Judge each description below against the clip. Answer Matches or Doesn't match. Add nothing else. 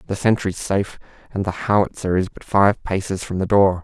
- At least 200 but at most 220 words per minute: Matches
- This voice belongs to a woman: Doesn't match